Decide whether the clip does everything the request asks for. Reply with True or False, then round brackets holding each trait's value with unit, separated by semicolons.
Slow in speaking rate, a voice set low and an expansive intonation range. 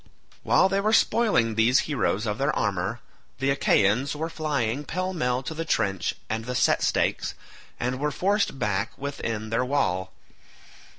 False (160 wpm; 125 Hz; 5.7 semitones)